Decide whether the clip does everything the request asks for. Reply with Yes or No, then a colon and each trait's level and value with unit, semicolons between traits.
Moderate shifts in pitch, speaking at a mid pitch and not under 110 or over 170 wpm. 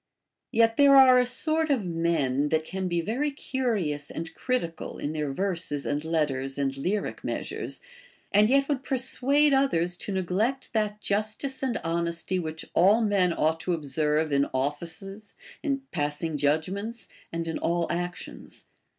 No: wide, 6.6 semitones; medium, 180 Hz; average, 155 wpm